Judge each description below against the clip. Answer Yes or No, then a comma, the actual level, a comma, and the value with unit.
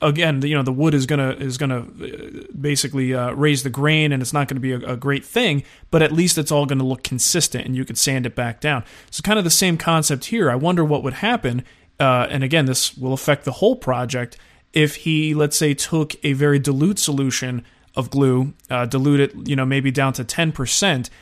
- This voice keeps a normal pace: No, fast, 230 wpm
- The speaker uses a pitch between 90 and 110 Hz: No, medium, 140 Hz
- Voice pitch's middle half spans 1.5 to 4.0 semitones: Yes, average, 2.8 semitones